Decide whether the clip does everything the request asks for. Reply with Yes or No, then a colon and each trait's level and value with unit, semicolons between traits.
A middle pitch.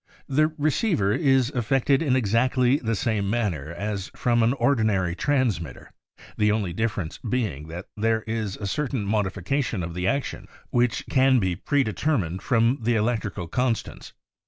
No: low, 110 Hz